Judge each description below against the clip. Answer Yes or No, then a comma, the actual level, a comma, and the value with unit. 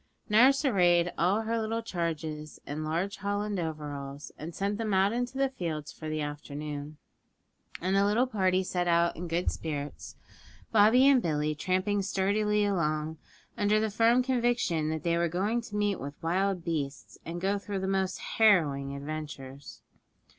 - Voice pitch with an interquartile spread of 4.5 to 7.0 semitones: Yes, average, 5.1 semitones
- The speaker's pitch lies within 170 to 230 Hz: Yes, medium, 185 Hz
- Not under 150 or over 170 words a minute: Yes, average, 160 wpm